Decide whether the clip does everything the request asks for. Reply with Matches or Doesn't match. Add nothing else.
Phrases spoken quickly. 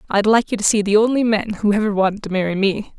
Matches